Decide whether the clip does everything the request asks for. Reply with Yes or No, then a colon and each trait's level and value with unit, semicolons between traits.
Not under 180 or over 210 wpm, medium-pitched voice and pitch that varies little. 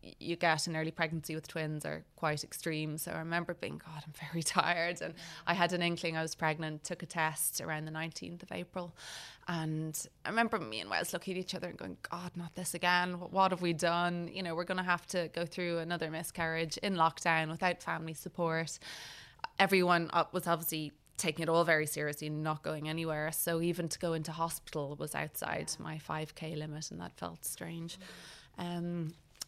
Yes: average, 200 wpm; medium, 165 Hz; narrow, 1.8 semitones